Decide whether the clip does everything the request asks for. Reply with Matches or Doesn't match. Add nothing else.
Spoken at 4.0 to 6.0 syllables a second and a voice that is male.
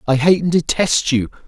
Matches